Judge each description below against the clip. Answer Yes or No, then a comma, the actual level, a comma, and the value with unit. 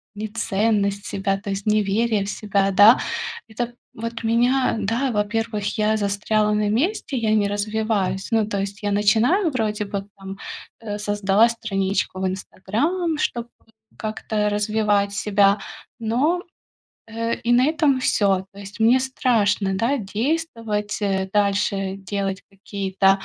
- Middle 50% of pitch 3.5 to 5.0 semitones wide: No, narrow, 2.4 semitones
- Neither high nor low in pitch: No, high, 210 Hz